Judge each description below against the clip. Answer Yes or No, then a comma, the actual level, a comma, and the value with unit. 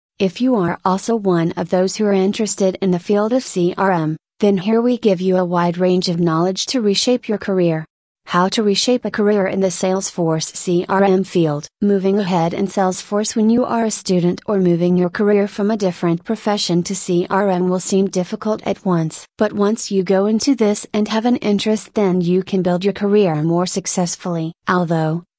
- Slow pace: No, average, 195 wpm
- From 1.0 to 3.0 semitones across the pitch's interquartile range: Yes, average, 2.7 semitones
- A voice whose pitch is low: No, high, 195 Hz